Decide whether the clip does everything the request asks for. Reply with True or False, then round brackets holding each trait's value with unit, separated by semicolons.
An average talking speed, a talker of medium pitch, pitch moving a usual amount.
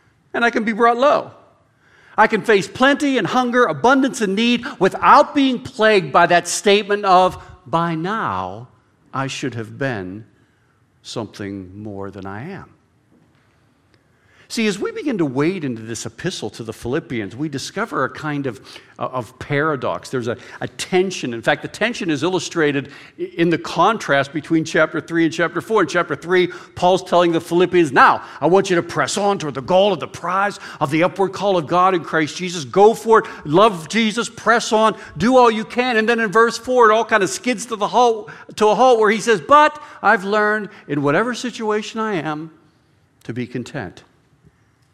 False (190 wpm; 180 Hz; 7.6 semitones)